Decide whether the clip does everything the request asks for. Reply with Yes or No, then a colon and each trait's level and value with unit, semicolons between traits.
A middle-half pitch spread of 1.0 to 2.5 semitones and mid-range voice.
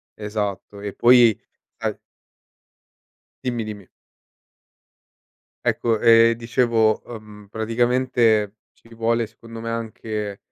No: narrow, 1.6 semitones; low, 115 Hz